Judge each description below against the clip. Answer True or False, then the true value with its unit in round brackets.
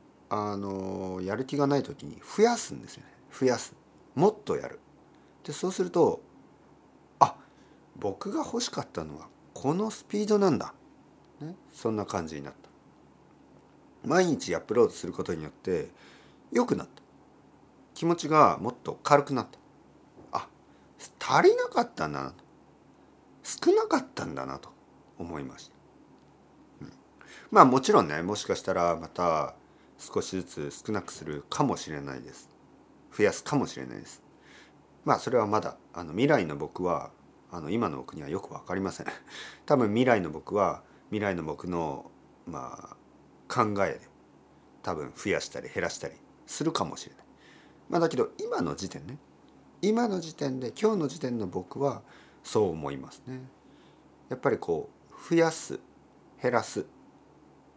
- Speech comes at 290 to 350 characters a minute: False (280 characters per minute)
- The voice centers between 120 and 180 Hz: True (135 Hz)